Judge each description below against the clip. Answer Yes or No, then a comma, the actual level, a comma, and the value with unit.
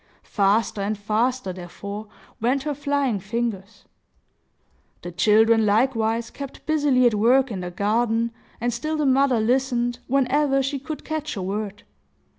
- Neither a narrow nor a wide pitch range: Yes, average, 4.3 semitones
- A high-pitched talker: Yes, high, 235 Hz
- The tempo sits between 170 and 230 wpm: No, average, 140 wpm